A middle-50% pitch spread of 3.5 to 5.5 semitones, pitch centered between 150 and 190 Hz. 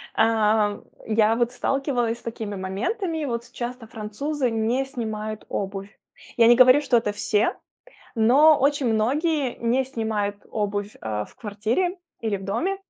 No: average, 3.8 semitones; high, 230 Hz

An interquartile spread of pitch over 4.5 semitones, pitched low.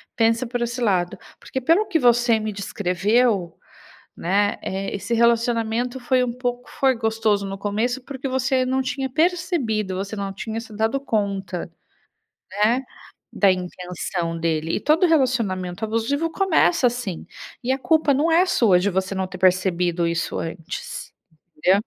No: average, 5.2 semitones; high, 225 Hz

